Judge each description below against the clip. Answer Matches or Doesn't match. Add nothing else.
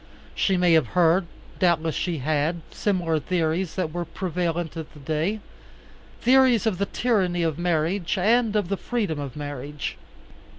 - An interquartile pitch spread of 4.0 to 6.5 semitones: Doesn't match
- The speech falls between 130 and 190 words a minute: Matches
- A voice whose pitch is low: Doesn't match